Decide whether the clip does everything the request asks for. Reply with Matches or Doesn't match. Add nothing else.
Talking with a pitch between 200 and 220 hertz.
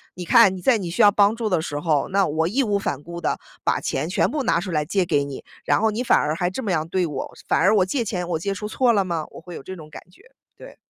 Doesn't match